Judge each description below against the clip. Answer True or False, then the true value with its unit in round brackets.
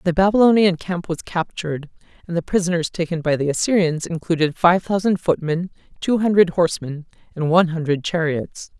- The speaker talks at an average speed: True (155 wpm)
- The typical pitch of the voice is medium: True (170 Hz)